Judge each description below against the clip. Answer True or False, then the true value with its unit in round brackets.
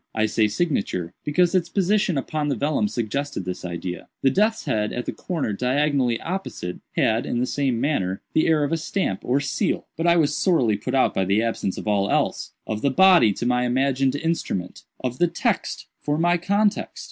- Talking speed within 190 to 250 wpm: True (195 wpm)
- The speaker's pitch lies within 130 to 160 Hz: True (135 Hz)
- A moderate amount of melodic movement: False (7.2 semitones)